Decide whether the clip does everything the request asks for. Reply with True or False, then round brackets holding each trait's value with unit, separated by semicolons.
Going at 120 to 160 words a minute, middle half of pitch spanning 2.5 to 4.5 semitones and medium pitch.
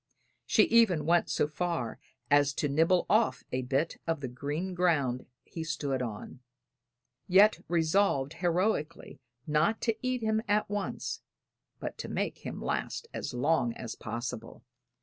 False (145 wpm; 5.5 semitones; 165 Hz)